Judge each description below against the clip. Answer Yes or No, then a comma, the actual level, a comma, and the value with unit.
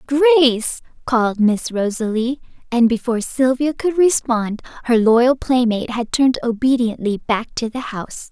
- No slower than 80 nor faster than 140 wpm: Yes, slow, 135 wpm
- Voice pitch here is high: Yes, high, 245 Hz